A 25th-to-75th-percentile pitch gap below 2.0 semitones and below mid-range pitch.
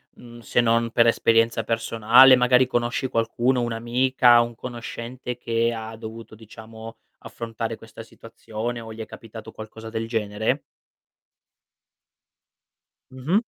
Yes: narrow, 1.2 semitones; low, 115 Hz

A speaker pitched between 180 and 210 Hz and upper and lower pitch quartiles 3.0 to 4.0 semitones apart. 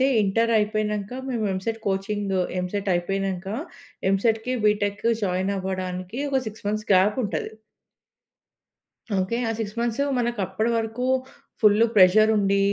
No: high, 205 Hz; narrow, 2.6 semitones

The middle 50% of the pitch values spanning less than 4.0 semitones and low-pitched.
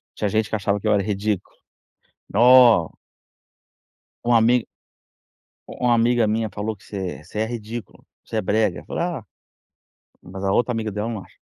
Yes: narrow, 2.6 semitones; low, 110 Hz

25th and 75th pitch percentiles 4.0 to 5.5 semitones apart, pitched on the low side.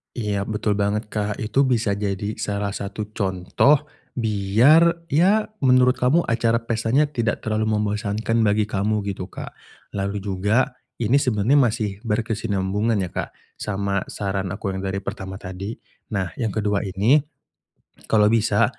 No: narrow, 2.6 semitones; low, 105 Hz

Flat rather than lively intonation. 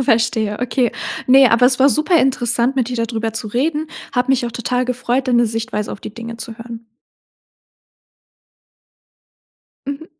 Yes: narrow, 2.3 semitones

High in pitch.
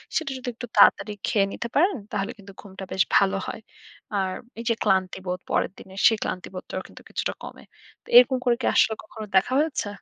Yes: high, 205 Hz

